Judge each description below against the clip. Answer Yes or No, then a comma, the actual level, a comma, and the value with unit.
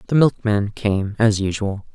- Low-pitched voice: Yes, low, 105 Hz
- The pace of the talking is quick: No, average, 155 wpm